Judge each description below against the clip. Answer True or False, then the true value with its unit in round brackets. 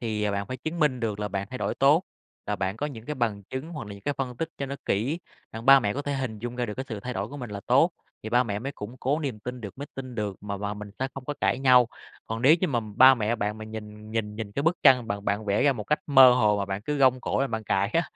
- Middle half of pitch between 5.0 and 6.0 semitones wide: False (4.4 semitones)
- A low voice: True (120 Hz)